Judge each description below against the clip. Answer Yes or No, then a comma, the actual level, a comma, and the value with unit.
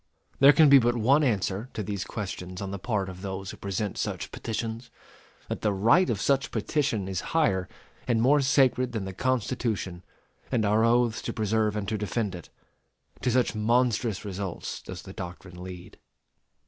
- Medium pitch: No, low, 110 Hz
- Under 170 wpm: No, average, 175 wpm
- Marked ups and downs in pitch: No, average, 4.2 semitones